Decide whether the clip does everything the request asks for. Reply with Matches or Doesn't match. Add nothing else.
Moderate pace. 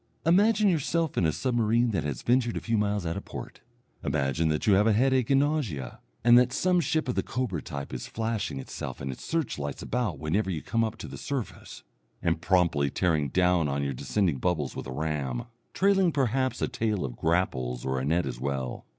Doesn't match